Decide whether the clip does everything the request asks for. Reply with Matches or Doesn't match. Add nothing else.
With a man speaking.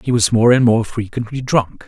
Matches